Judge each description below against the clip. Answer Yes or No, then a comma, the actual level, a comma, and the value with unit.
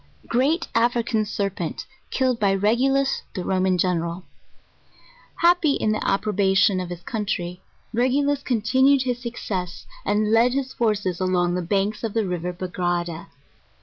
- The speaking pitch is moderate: No, high, 210 Hz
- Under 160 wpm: Yes, average, 145 wpm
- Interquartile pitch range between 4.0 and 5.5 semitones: Yes, average, 5.2 semitones